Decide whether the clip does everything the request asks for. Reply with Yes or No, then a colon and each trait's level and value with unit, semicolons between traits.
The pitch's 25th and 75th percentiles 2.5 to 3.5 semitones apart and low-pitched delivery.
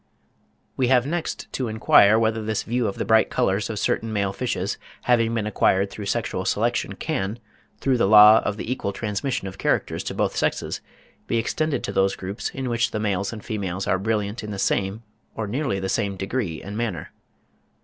Yes: average, 3.0 semitones; low, 110 Hz